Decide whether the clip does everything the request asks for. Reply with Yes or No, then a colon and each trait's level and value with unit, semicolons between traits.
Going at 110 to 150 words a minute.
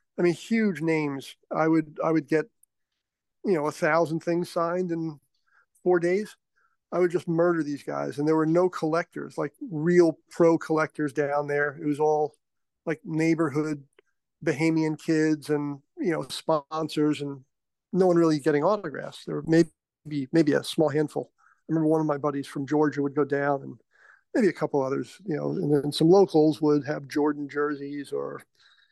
No: average, 180 wpm